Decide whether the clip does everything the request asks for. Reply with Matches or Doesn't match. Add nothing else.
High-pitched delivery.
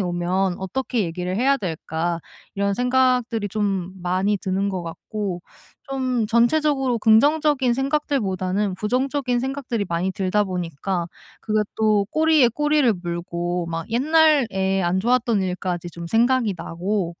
Matches